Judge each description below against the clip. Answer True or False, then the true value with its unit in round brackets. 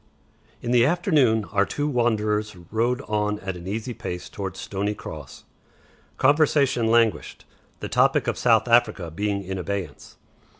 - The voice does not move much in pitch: False (3.5 semitones)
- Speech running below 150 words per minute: True (140 wpm)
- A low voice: True (110 Hz)